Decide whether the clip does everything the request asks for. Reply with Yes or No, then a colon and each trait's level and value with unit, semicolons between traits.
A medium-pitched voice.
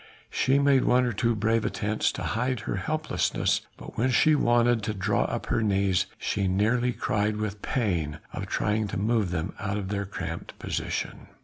No: low, 105 Hz